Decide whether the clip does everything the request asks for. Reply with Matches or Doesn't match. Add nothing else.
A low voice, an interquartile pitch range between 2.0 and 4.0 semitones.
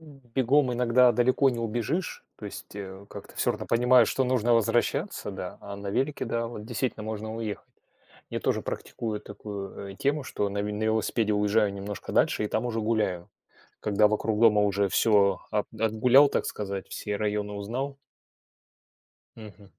Matches